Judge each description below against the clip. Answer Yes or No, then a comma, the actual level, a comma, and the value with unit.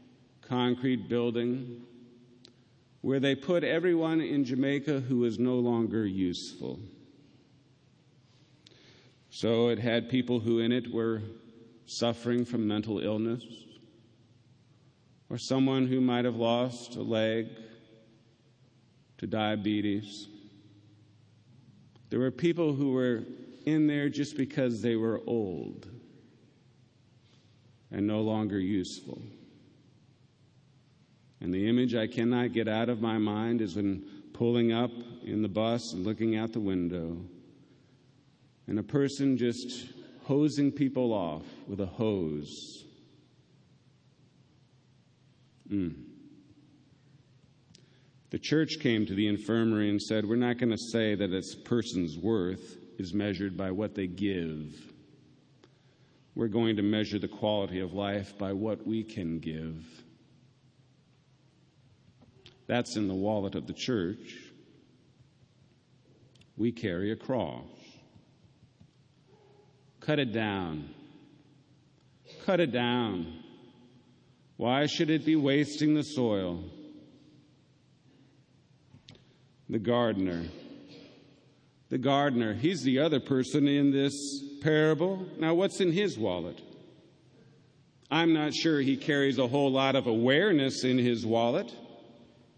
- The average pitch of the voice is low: Yes, low, 125 Hz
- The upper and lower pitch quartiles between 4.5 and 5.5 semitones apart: No, average, 3.6 semitones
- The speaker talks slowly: Yes, slow, 110 wpm